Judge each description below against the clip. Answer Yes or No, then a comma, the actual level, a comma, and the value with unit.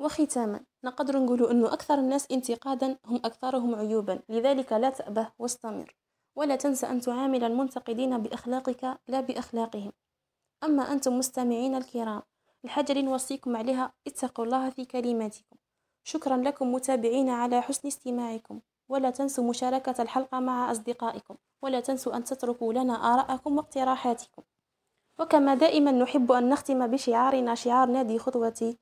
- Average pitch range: No, narrow, 2.0 semitones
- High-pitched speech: Yes, very high, 255 Hz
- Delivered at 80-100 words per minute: No, average, 125 wpm